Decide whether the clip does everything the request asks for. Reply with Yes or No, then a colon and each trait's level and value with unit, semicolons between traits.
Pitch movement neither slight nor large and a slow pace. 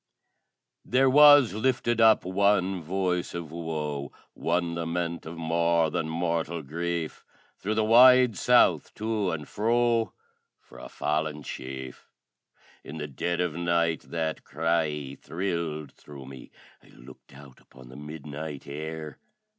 Yes: average, 4.1 semitones; slow, 130 wpm